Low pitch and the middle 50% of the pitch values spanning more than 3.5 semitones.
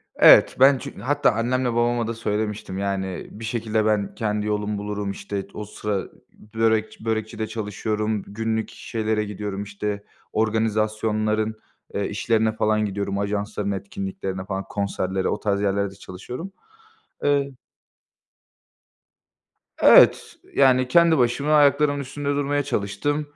No: low, 110 Hz; average, 2.8 semitones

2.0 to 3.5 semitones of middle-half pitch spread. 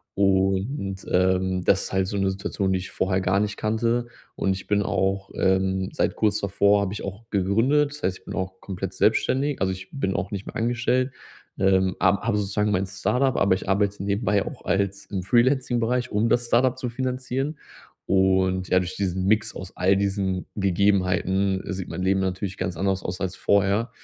Yes: narrow, 2.6 semitones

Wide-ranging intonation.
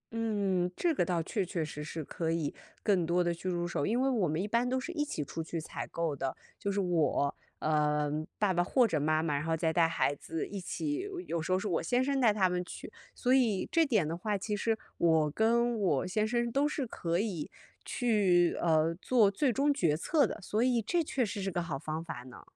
Yes: wide, 6.1 semitones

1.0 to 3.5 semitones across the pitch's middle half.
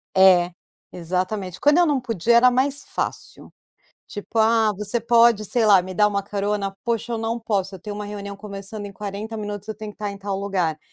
Yes: narrow, 2.4 semitones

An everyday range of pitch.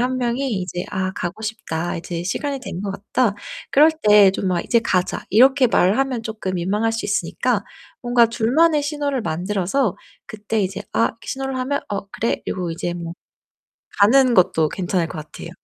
No: wide, 5.8 semitones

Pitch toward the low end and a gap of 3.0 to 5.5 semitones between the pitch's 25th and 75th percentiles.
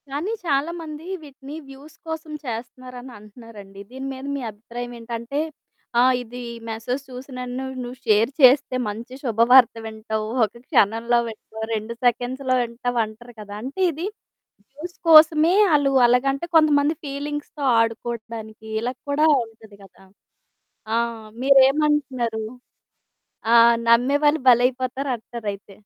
No: very high, 250 Hz; average, 3.6 semitones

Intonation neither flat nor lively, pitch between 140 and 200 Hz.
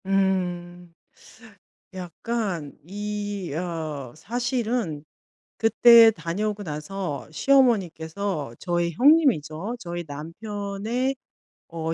Yes: average, 4.9 semitones; high, 190 Hz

